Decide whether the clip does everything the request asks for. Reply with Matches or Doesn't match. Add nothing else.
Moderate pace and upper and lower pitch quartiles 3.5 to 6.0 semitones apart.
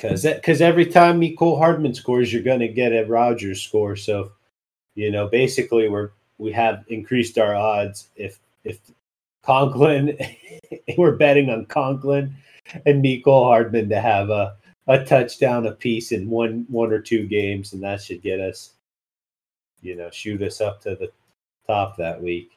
Matches